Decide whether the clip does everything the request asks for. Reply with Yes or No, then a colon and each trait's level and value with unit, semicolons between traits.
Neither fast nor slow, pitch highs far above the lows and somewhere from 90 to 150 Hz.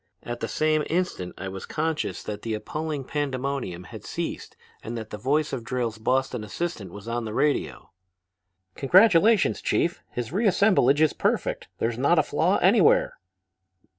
Yes: average, 155 wpm; wide, 6.1 semitones; low, 135 Hz